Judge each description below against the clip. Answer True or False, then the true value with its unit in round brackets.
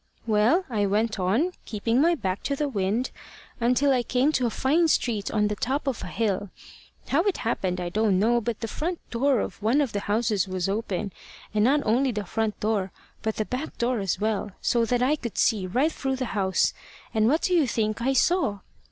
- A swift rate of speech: True (215 wpm)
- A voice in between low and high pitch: False (230 Hz)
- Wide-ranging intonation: False (4.3 semitones)